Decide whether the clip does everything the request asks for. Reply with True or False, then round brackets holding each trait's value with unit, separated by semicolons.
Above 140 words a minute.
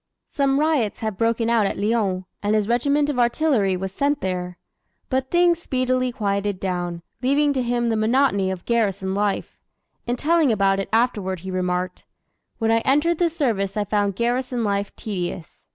True (170 wpm)